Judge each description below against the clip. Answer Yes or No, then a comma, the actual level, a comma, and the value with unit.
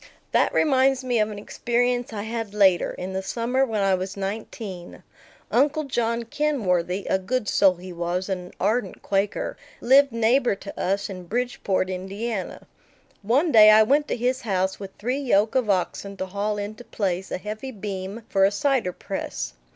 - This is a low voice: No, high, 210 Hz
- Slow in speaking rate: No, average, 175 wpm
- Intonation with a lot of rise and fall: No, average, 4.2 semitones